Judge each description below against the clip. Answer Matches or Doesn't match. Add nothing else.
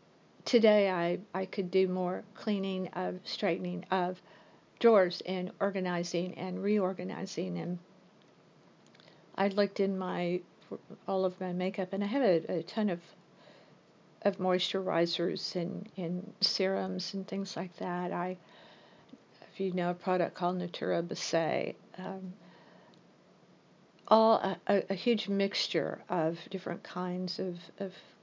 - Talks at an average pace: Doesn't match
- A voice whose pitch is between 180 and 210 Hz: Matches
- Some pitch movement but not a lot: Doesn't match